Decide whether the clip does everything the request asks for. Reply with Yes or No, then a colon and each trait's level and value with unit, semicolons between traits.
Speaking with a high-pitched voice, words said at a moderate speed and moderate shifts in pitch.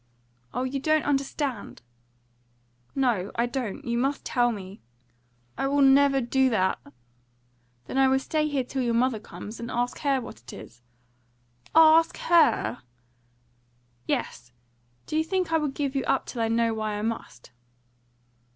Yes: very high, 260 Hz; average, 155 wpm; average, 3.7 semitones